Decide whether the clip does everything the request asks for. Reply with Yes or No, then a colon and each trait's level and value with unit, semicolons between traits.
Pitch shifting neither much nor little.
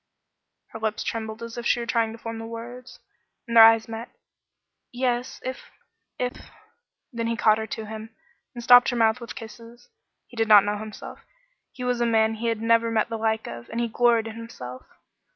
No: narrow, 1.3 semitones